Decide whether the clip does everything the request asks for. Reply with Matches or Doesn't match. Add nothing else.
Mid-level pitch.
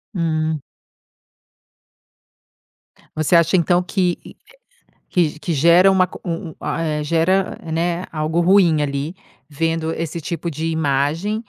Matches